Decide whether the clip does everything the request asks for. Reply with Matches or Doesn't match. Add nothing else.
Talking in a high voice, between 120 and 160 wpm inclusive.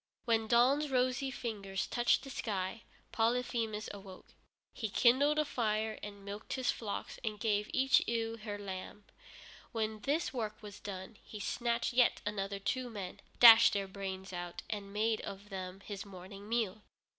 Matches